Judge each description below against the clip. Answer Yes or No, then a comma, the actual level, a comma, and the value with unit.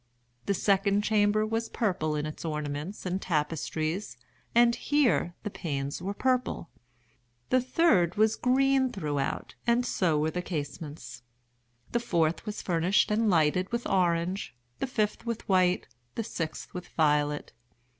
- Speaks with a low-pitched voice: No, medium, 185 Hz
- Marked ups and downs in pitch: Yes, wide, 5.8 semitones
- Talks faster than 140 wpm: No, slow, 135 wpm